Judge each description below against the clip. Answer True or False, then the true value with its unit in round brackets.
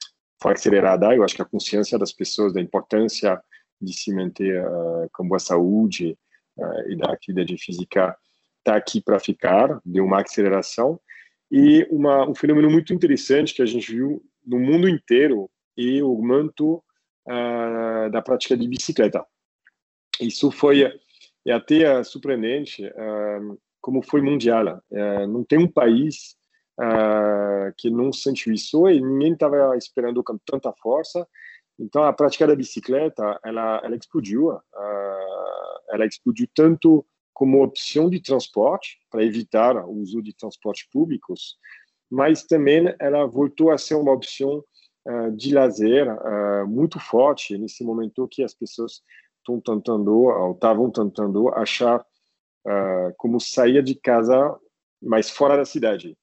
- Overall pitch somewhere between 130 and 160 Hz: False (120 Hz)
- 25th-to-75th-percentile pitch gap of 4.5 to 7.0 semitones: True (5.3 semitones)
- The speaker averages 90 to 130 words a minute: False (145 wpm)